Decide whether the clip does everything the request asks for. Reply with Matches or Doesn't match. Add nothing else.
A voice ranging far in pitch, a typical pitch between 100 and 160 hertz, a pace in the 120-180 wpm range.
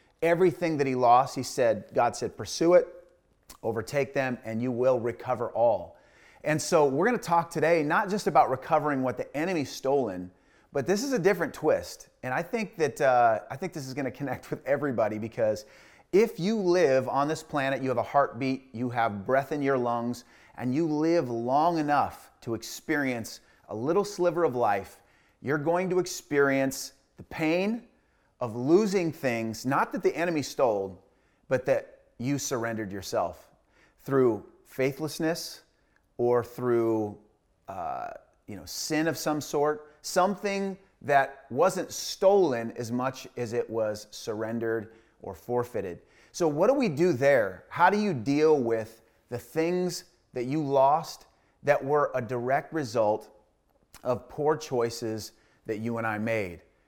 Matches